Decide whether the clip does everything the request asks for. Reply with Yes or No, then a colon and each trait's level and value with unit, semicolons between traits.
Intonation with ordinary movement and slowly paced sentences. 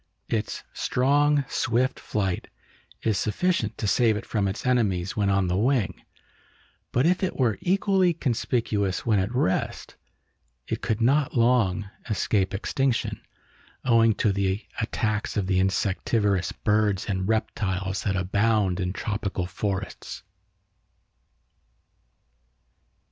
Yes: average, 4.0 semitones; slow, 120 wpm